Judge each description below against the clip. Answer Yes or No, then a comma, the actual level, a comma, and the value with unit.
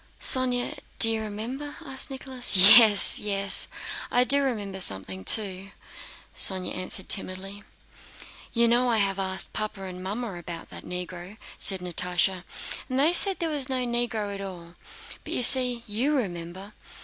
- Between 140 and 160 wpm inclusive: Yes, average, 150 wpm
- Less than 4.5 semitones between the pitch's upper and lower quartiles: No, average, 4.8 semitones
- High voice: Yes, high, 210 Hz